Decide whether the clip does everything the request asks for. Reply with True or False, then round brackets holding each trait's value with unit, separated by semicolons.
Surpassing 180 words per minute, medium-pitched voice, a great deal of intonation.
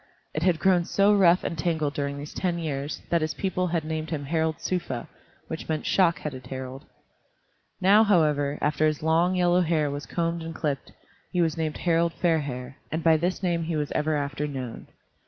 False (190 wpm; 160 Hz; 2.7 semitones)